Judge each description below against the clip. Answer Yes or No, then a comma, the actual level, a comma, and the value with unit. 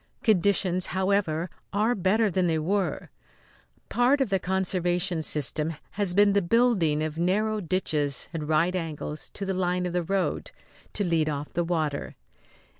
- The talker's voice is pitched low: No, medium, 180 Hz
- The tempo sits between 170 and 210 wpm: No, average, 155 wpm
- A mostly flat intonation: No, average, 3.7 semitones